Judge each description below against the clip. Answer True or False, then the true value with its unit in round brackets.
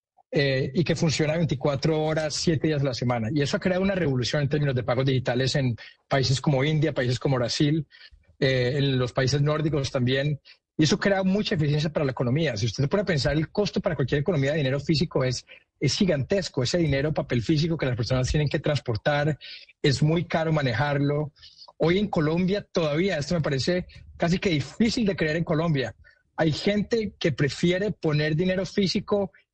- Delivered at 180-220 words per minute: True (190 wpm)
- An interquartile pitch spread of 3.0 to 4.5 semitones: True (4.1 semitones)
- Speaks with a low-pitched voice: False (155 Hz)